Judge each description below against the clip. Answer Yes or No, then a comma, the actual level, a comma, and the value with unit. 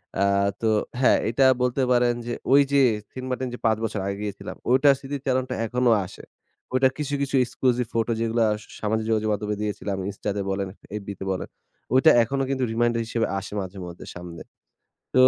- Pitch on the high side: No, low, 115 Hz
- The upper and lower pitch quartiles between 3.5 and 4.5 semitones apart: Yes, average, 3.8 semitones